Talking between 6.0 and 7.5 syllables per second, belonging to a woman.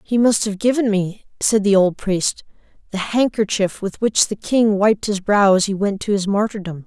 No: 4.7 syllables/s; female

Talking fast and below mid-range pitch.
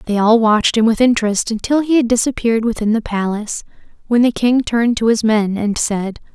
No: fast, 210 wpm; high, 225 Hz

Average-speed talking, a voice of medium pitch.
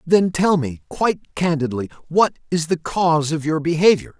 Yes: average, 170 wpm; medium, 160 Hz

